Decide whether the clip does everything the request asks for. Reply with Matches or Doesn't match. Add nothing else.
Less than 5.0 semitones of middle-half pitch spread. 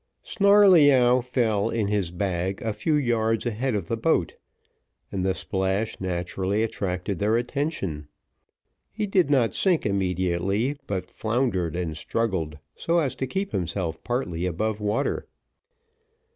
Doesn't match